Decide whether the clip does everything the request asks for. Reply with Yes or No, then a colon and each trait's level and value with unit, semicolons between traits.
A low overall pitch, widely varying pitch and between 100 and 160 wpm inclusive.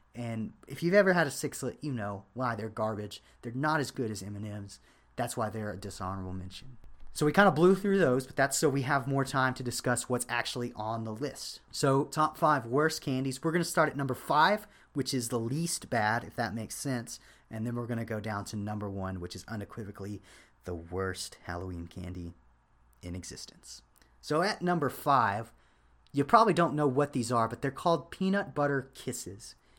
No: low, 120 Hz; wide, 5.9 semitones; fast, 205 wpm